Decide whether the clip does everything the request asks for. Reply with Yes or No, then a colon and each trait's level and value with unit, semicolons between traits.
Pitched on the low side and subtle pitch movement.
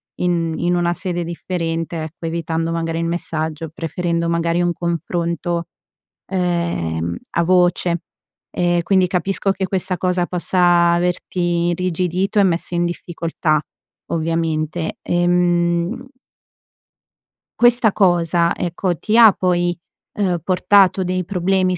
No: medium, 175 Hz; narrow, 1.4 semitones